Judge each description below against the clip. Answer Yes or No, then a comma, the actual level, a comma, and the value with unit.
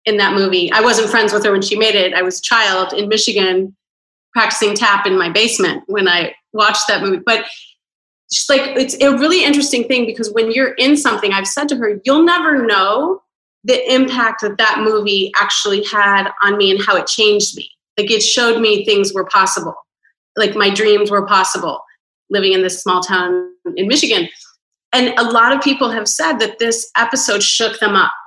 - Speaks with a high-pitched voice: Yes, high, 215 Hz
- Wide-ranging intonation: No, average, 3.8 semitones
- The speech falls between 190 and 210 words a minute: Yes, average, 195 wpm